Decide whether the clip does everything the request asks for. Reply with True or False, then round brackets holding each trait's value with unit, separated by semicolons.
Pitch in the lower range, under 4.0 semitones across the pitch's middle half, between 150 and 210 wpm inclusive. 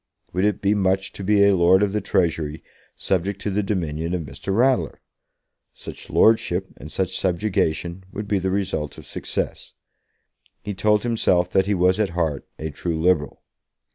True (95 Hz; 3.0 semitones; 170 wpm)